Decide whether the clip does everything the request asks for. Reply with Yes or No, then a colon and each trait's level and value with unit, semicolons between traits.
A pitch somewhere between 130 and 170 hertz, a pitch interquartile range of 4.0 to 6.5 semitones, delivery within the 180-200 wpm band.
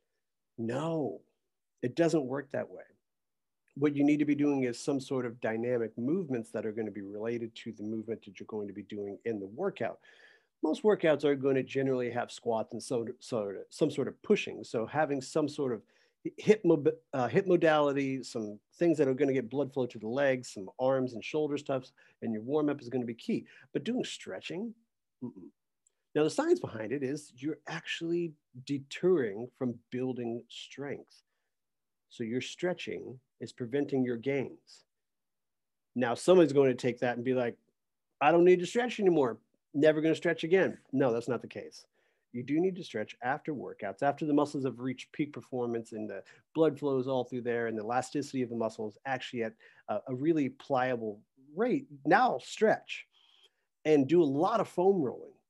Yes: low, 135 Hz; average, 4.6 semitones; average, 195 wpm